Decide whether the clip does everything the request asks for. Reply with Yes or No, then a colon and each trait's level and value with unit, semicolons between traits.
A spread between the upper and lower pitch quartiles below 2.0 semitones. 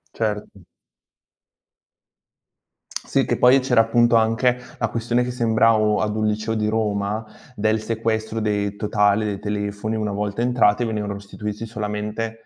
Yes: narrow, 1.4 semitones